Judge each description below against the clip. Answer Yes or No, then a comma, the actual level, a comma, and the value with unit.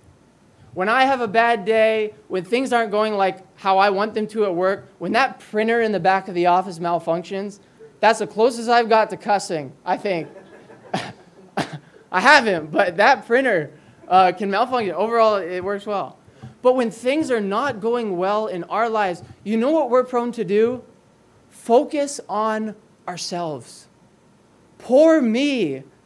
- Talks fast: No, average, 165 wpm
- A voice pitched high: Yes, high, 215 Hz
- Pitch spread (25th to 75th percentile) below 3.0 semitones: No, average, 3.8 semitones